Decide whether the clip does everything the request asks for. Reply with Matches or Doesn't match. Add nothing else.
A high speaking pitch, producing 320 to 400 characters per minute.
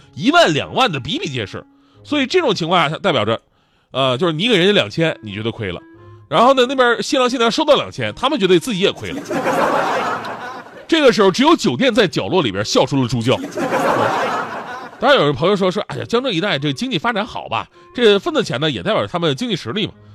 Matches